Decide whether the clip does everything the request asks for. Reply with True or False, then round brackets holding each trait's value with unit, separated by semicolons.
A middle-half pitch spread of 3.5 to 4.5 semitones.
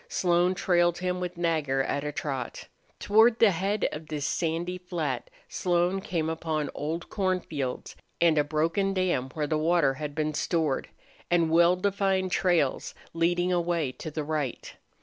False (2.9 semitones)